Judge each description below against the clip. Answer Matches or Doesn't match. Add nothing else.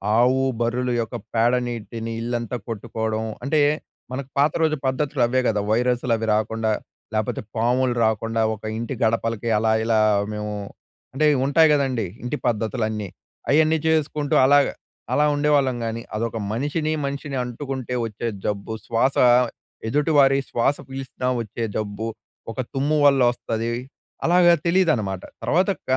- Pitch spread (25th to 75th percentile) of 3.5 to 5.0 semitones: Matches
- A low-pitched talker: Matches